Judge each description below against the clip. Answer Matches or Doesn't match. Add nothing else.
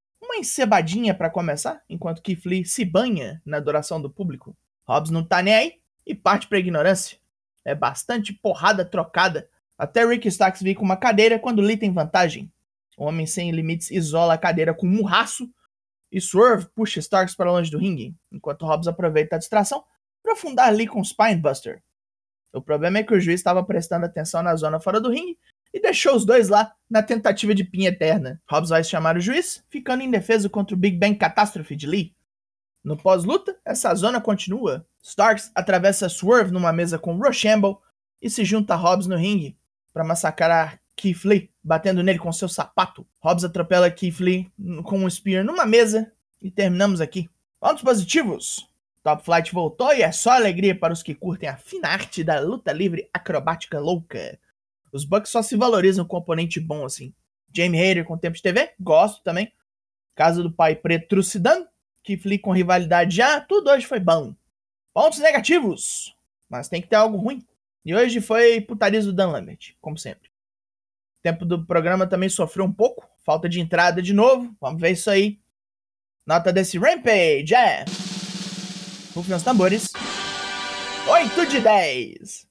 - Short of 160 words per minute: Doesn't match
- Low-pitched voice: Doesn't match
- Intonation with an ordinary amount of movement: Matches